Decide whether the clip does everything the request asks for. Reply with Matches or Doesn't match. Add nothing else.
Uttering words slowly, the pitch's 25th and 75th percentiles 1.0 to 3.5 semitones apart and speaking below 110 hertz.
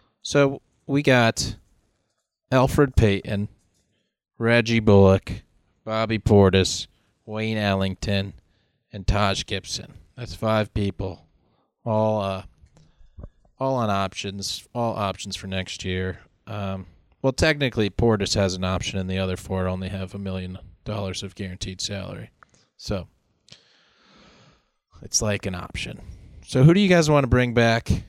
Matches